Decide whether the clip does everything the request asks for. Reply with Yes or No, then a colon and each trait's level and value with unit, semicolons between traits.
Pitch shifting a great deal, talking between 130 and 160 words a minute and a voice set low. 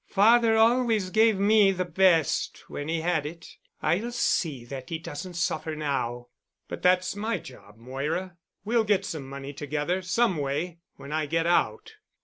No: wide, 5.7 semitones; average, 150 wpm; medium, 175 Hz